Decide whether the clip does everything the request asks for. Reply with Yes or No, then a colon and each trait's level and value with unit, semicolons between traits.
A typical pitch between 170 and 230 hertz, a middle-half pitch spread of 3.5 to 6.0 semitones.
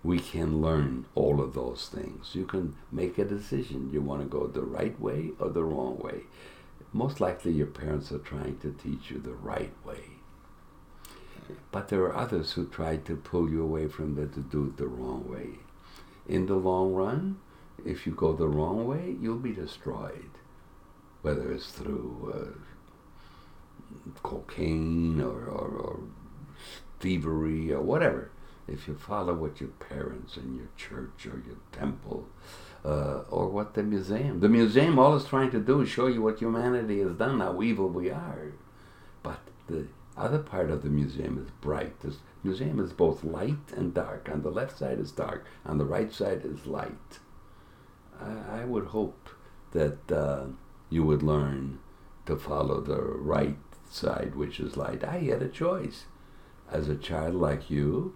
No: very low, 80 Hz; average, 5.0 semitones